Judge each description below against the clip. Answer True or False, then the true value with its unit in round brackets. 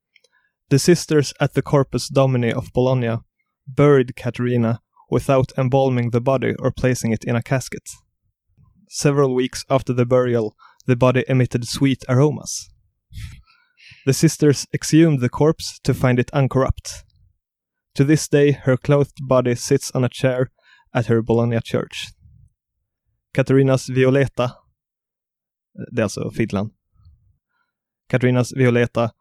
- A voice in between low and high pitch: False (130 Hz)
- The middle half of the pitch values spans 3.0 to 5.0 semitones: False (2.5 semitones)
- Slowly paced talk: True (120 wpm)